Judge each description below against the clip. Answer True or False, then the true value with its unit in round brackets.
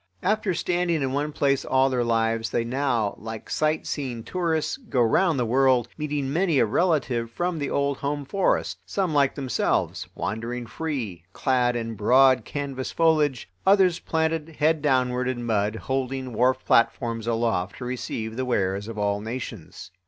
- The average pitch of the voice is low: True (130 Hz)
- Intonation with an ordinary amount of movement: True (4.6 semitones)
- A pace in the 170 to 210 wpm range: False (160 wpm)